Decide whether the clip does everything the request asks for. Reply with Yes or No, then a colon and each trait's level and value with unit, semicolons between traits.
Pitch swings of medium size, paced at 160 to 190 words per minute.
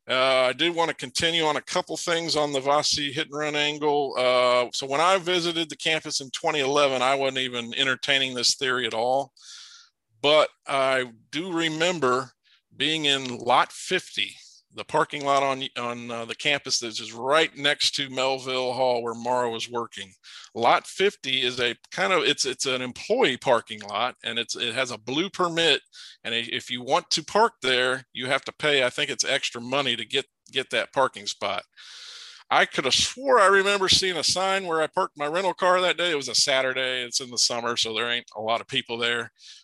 No: average, 4.5 semitones; fast, 205 wpm